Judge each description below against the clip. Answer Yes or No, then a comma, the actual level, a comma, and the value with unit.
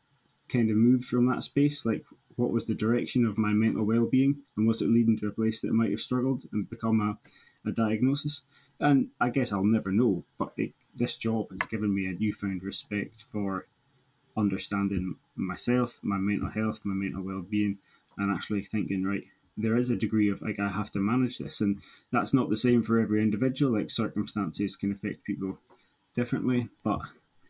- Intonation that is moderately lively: Yes, average, 3.2 semitones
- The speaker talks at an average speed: Yes, average, 190 wpm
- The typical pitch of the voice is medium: No, low, 110 Hz